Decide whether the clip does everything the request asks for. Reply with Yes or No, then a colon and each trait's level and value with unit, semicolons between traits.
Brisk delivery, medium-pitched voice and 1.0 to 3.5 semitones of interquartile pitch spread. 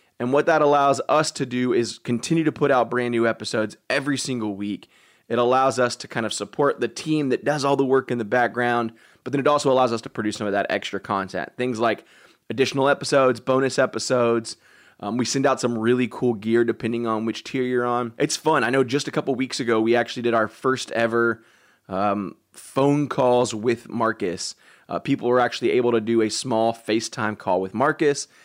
No: fast, 215 wpm; low, 125 Hz; average, 2.9 semitones